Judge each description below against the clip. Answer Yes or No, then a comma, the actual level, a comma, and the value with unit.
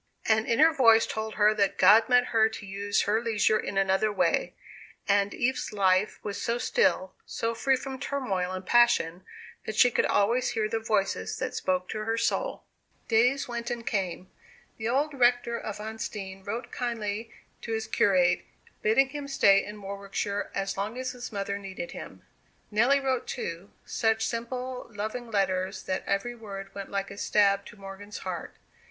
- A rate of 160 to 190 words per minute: Yes, average, 170 wpm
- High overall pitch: Yes, high, 215 Hz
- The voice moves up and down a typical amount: Yes, average, 3.4 semitones